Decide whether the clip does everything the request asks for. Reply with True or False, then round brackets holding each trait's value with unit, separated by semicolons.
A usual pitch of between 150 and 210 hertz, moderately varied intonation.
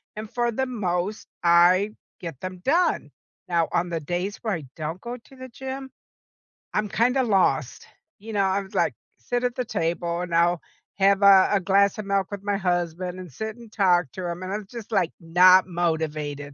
True (190 Hz; 3.7 semitones)